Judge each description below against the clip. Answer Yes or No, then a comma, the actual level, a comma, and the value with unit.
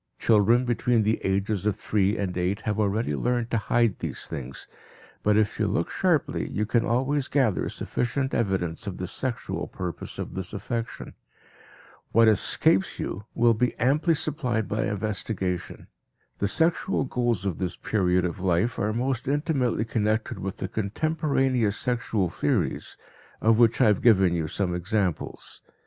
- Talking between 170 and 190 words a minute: No, average, 155 wpm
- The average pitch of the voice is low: Yes, low, 110 Hz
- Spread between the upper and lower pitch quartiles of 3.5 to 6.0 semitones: Yes, average, 4.0 semitones